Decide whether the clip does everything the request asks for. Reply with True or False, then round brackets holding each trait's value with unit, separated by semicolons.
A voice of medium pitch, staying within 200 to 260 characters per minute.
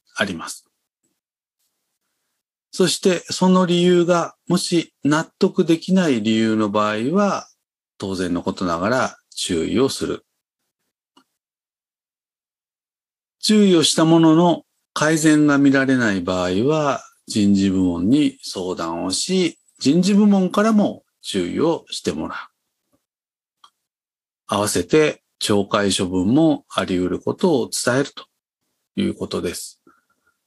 True (155 Hz; 215 characters per minute)